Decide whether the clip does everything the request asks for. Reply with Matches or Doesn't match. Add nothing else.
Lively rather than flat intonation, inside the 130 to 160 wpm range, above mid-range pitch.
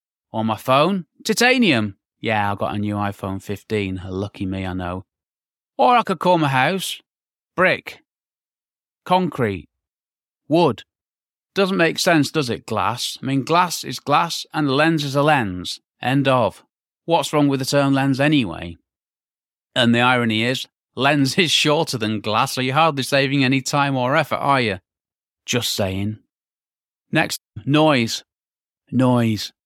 Doesn't match